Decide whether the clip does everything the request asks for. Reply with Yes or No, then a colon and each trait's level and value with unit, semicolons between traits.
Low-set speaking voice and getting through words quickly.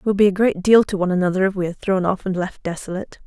No: high, 190 Hz; fast, 295 wpm